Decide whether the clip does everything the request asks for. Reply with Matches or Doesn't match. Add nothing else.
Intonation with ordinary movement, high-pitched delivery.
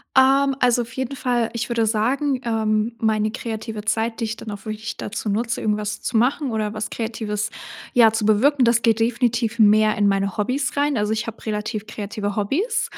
Doesn't match